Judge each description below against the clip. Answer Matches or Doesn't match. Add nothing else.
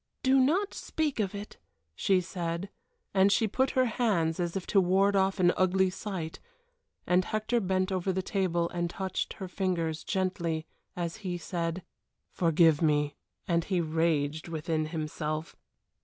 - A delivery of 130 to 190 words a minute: Matches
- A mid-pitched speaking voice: Matches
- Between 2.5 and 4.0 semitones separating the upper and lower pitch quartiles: Matches